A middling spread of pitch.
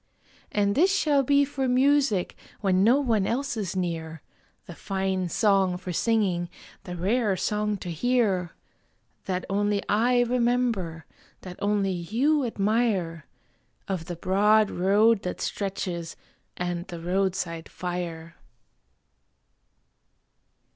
Yes: average, 4.5 semitones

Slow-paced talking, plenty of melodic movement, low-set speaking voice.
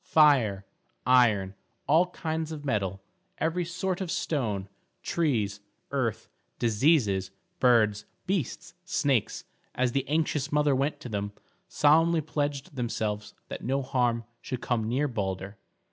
Yes: slow, 125 wpm; wide, 6.3 semitones; low, 130 Hz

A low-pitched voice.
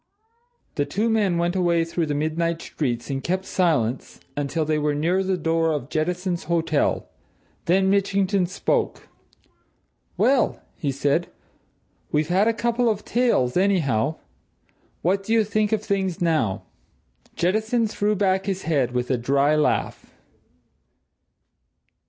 No: medium, 175 Hz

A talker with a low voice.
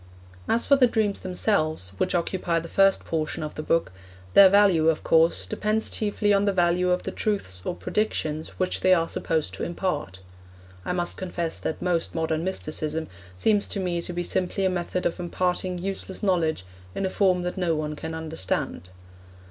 No: medium, 175 Hz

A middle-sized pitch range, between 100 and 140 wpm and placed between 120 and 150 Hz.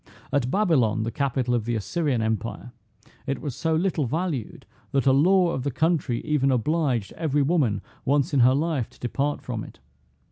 No: average, 4.7 semitones; average, 180 wpm; medium, 140 Hz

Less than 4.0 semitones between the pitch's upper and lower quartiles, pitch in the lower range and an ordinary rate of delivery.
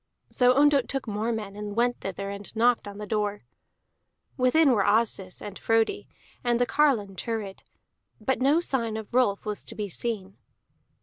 No: average, 3.4 semitones; high, 225 Hz; average, 170 wpm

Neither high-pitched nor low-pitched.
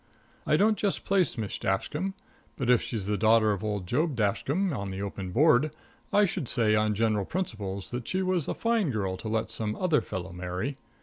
No: low, 115 Hz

